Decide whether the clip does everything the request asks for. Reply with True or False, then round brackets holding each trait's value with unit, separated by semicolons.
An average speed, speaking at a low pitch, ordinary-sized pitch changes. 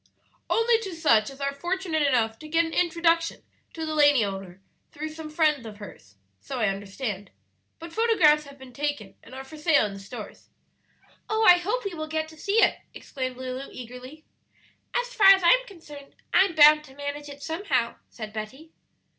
False (190 wpm; 295 Hz; 4.9 semitones)